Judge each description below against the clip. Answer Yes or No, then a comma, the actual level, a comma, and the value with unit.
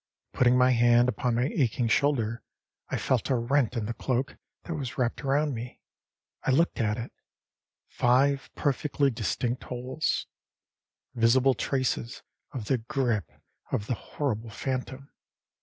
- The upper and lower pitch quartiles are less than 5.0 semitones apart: Yes, narrow, 2.6 semitones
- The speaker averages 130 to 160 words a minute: Yes, average, 140 wpm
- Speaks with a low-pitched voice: Yes, low, 125 Hz